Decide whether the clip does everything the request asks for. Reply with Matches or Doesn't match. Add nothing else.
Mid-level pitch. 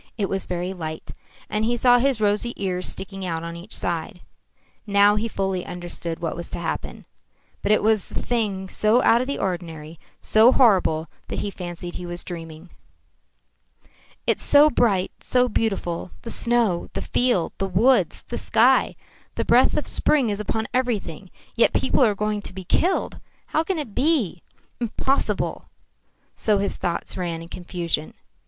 Doesn't match